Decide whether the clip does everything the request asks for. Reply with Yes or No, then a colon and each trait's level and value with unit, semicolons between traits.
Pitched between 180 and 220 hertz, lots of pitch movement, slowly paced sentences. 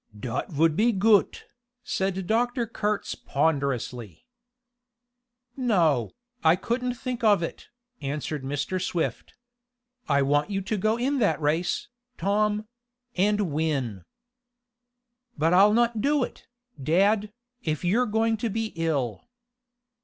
Yes: high, 190 Hz; wide, 6.5 semitones; slow, 120 wpm